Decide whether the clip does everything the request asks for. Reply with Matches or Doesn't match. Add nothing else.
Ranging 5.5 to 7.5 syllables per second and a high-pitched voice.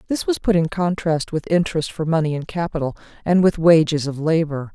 Doesn't match